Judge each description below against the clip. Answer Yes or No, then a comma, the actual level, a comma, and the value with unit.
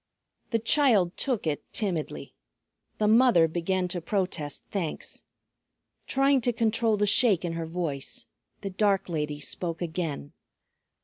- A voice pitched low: No, medium, 185 Hz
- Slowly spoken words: Yes, slow, 130 wpm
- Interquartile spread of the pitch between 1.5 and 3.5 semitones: No, average, 5.3 semitones